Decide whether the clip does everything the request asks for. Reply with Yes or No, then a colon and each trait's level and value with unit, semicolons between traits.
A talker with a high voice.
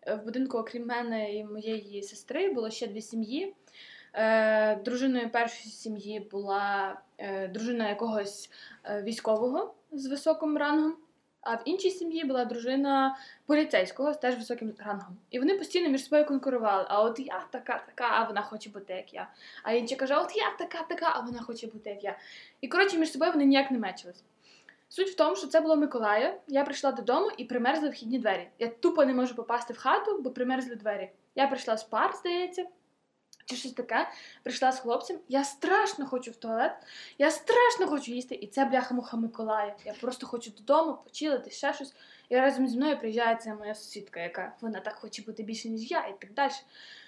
Yes: very high, 250 Hz